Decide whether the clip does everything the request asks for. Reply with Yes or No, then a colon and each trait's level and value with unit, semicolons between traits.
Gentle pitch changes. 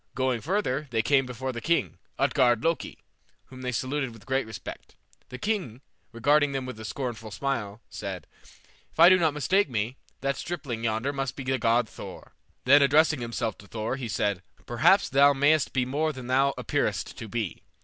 No: average, 3.6 semitones